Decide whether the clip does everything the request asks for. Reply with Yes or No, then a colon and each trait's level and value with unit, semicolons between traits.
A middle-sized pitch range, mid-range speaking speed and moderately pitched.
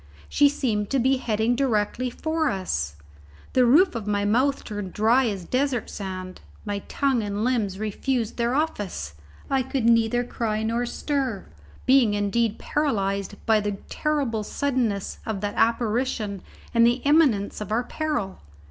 No: average, 4.2 semitones; average, 150 wpm; high, 230 Hz